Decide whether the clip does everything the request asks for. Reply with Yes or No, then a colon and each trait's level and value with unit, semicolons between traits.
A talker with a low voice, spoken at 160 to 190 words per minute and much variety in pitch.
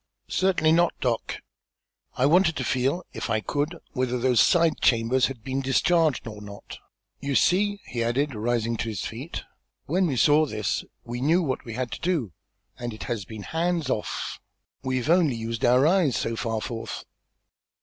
Yes: low, 130 Hz; average, 175 wpm; wide, 5.7 semitones